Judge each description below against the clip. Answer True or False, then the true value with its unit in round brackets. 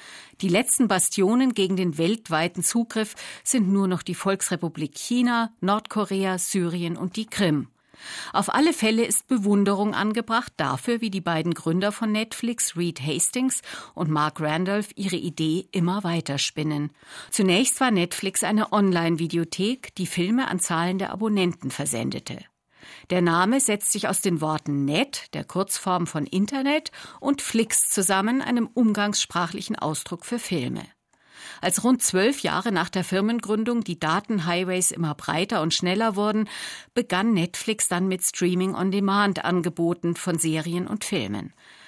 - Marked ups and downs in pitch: False (4.2 semitones)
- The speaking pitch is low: False (190 Hz)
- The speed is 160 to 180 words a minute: False (140 wpm)